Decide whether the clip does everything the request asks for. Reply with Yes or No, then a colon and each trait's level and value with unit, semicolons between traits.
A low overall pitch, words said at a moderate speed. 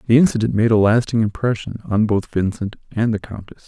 Yes: low, 110 Hz; average, 195 wpm